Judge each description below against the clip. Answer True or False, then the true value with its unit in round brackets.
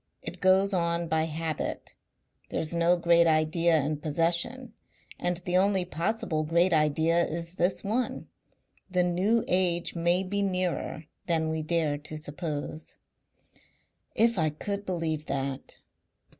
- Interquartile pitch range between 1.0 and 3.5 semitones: True (2.6 semitones)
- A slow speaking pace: True (130 wpm)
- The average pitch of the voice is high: False (170 Hz)